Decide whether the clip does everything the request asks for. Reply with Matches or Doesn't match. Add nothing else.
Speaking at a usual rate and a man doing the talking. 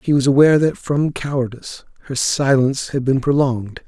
Matches